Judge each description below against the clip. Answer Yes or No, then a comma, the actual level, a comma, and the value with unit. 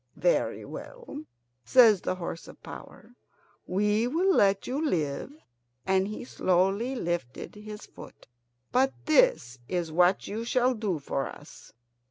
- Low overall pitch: No, high, 210 Hz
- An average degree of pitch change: No, wide, 6.1 semitones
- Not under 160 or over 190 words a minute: No, slow, 135 wpm